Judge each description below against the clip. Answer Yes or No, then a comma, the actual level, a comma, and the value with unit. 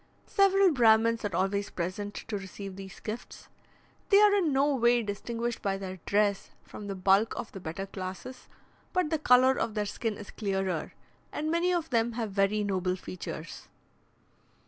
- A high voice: Yes, high, 210 Hz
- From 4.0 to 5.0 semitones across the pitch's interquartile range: Yes, average, 4.4 semitones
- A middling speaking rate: Yes, average, 170 wpm